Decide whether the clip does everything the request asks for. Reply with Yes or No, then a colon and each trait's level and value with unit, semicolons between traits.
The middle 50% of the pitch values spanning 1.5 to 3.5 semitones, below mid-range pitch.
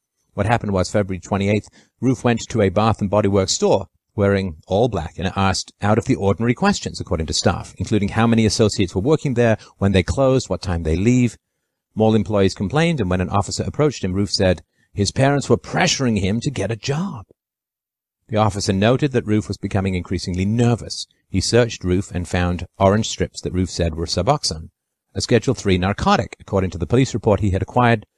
No: average, 3.9 semitones; low, 100 Hz